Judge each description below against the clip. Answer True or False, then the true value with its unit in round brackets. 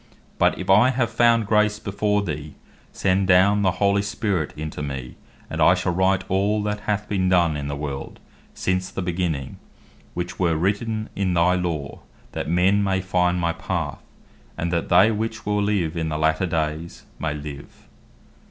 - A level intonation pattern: False (3.9 semitones)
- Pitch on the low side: True (95 Hz)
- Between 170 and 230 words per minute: True (175 wpm)